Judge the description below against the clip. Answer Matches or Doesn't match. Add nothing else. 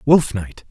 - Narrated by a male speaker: Matches